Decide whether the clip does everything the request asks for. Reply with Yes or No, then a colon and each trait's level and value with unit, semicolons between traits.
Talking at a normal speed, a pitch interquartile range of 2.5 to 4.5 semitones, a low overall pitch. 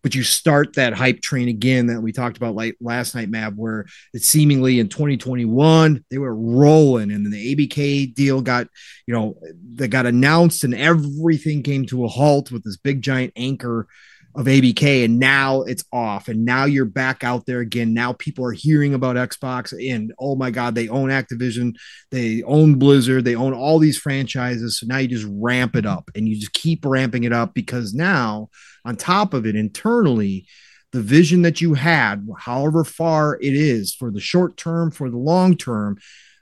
Yes: average, 195 wpm; average, 3.2 semitones; low, 130 Hz